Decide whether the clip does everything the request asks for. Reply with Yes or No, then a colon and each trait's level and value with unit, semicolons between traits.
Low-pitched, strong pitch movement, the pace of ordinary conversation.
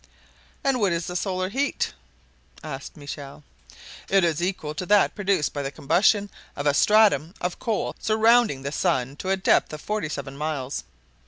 No: medium, 175 Hz; wide, 6.0 semitones; average, 170 wpm